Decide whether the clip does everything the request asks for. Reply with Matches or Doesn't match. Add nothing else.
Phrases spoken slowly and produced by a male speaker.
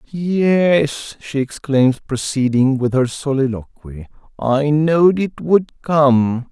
Matches